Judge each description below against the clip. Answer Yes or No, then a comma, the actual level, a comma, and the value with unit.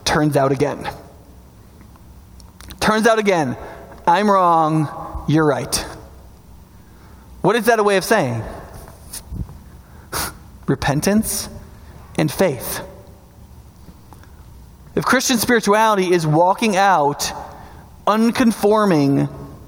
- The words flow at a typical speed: No, slow, 80 wpm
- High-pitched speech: No, medium, 155 Hz